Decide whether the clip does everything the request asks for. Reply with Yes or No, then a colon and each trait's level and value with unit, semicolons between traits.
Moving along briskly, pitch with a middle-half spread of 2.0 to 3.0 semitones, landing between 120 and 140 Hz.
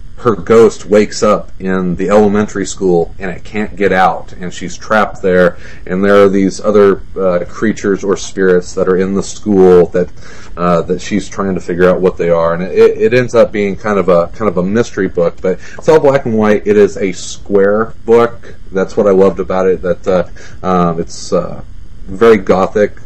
No: fast, 210 wpm; narrow, 2.5 semitones; very low, 95 Hz